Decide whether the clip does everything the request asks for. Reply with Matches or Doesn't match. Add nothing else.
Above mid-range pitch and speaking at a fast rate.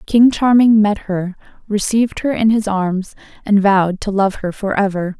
Doesn't match